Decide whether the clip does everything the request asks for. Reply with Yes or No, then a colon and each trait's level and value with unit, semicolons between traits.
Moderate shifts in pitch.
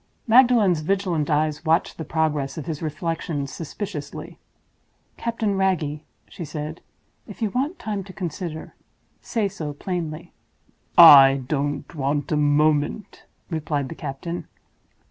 Yes: average, 4.5 semitones